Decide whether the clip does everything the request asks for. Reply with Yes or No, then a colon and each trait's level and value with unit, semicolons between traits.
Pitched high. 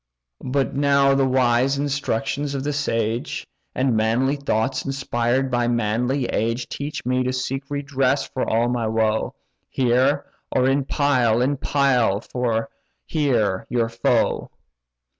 No: low, 130 Hz